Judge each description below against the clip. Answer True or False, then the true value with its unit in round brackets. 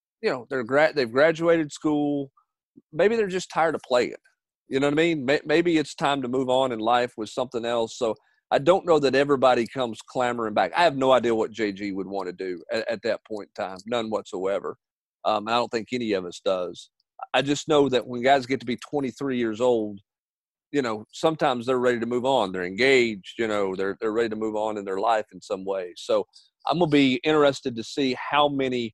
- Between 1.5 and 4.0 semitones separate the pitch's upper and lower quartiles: False (4.4 semitones)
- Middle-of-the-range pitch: False (125 Hz)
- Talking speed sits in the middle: False (225 wpm)